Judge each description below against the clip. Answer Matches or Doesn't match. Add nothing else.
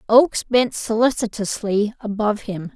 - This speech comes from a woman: Matches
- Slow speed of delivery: Matches